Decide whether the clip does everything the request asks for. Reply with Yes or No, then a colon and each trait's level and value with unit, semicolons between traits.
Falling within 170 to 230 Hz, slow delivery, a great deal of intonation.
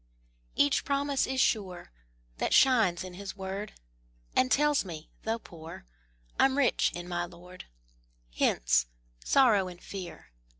Yes: high, 190 Hz; slow, 130 wpm; wide, 6.6 semitones